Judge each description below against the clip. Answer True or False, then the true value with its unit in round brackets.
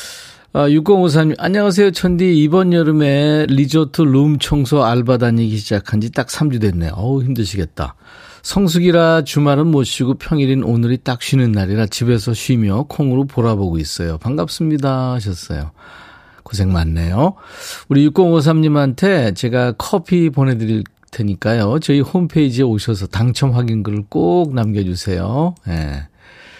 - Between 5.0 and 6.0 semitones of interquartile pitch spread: False (6.5 semitones)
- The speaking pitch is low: True (130 Hz)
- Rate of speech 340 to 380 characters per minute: False (300 characters per minute)